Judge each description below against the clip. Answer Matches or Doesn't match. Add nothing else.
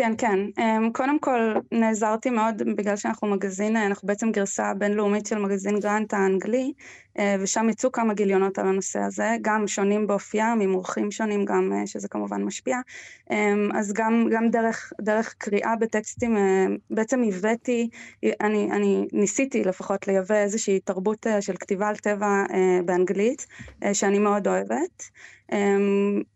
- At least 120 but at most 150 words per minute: Matches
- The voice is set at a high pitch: Matches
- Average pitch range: Doesn't match